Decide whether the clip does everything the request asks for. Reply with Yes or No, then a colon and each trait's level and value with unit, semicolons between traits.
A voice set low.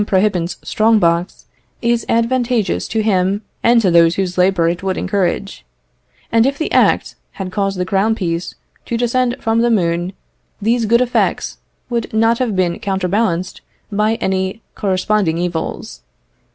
No: high, 200 Hz